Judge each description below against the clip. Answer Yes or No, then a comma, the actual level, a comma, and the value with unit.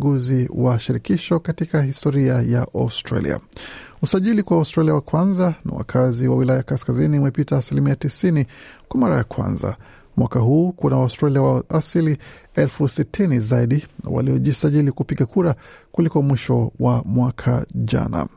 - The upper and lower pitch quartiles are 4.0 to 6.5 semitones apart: No, average, 3.5 semitones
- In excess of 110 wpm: Yes, average, 135 wpm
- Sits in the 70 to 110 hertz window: No, medium, 140 Hz